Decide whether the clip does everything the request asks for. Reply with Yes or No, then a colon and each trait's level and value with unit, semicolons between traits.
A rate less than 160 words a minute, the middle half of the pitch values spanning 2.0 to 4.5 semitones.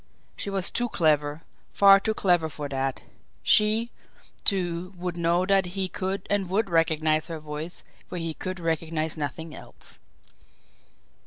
Yes: average, 145 wpm; average, 3.6 semitones